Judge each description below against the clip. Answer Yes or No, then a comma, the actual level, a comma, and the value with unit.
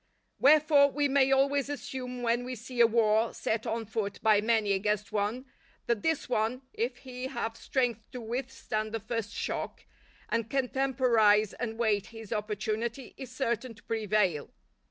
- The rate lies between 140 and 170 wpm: Yes, average, 160 wpm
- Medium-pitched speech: No, high, 230 Hz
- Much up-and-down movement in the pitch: No, average, 3.0 semitones